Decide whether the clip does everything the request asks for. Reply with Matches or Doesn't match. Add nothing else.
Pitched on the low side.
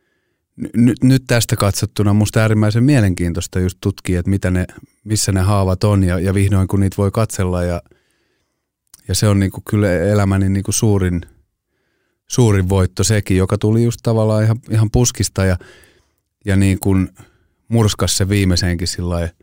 Matches